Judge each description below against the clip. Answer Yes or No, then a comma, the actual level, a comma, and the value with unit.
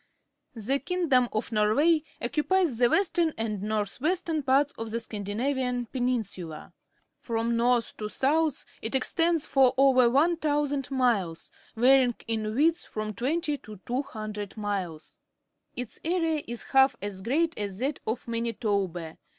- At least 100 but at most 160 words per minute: Yes, average, 140 wpm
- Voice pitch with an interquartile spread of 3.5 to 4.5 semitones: No, average, 5.2 semitones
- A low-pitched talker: No, high, 245 Hz